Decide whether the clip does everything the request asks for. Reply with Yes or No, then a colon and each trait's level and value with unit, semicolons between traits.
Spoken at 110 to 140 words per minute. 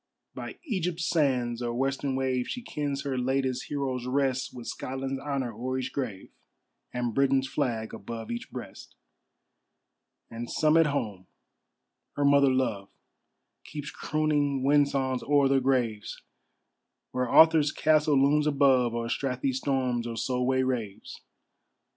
Yes: slow, 135 wpm